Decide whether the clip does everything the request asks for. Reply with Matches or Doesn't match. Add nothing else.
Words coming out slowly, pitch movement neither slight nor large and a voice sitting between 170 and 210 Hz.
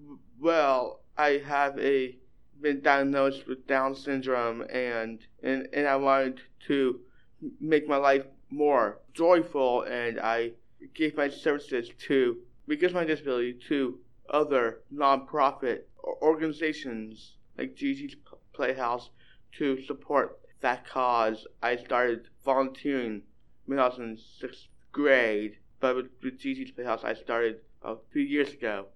Doesn't match